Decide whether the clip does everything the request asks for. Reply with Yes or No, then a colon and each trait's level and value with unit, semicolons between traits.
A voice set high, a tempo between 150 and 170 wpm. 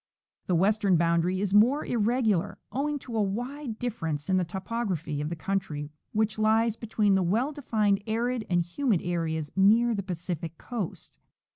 Yes: high, 205 Hz; average, 165 wpm